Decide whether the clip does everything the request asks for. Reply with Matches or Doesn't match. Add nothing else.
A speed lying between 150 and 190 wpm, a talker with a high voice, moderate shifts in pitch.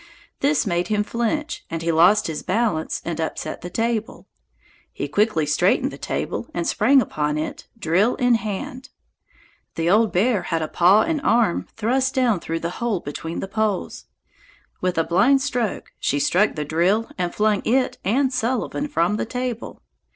Doesn't match